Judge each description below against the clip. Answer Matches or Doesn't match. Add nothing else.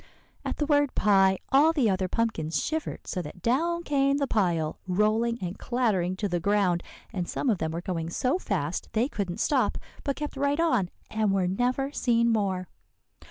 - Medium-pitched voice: Doesn't match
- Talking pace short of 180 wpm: Doesn't match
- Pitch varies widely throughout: Matches